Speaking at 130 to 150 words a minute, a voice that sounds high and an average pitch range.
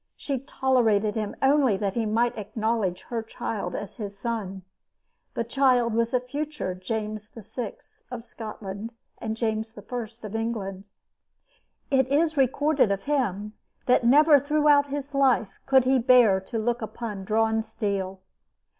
Yes: average, 145 wpm; high, 230 Hz; average, 3.8 semitones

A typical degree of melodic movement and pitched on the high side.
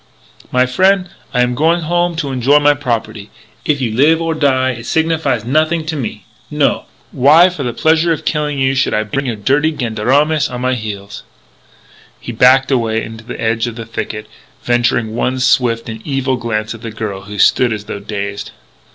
No: average, 4.9 semitones; low, 125 Hz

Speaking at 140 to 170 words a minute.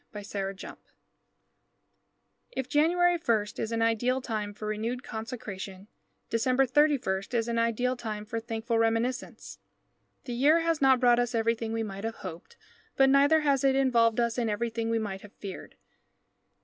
Yes: average, 160 wpm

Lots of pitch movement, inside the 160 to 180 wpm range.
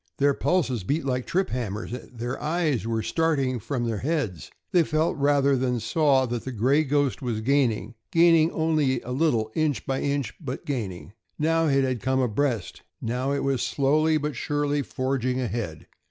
No: average, 3.5 semitones; average, 170 wpm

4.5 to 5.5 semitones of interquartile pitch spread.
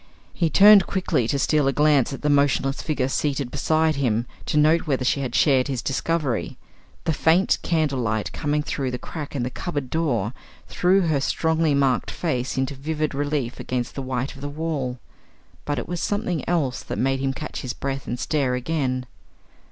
No: average, 3.4 semitones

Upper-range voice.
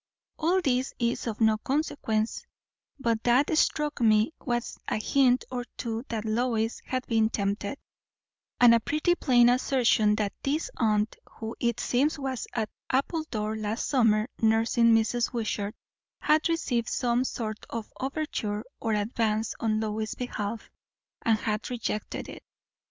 Yes: high, 230 Hz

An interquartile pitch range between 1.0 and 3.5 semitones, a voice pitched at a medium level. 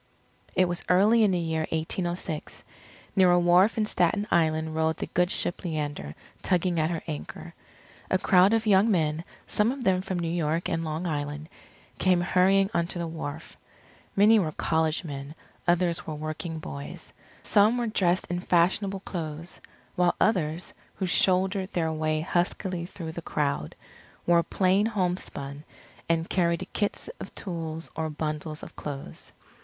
Yes: average, 2.9 semitones; medium, 175 Hz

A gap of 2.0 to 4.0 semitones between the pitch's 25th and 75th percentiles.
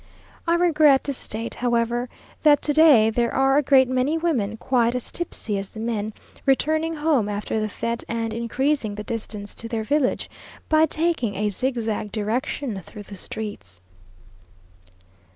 No: average, 4.9 semitones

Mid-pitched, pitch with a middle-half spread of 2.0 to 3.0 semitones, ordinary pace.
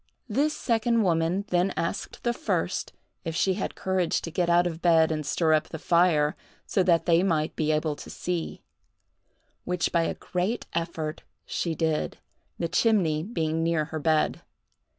Yes: medium, 170 Hz; narrow, 2.5 semitones; average, 170 wpm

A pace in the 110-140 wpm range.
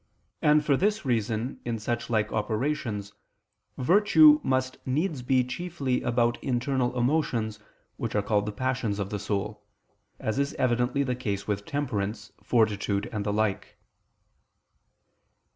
Yes: slow, 135 wpm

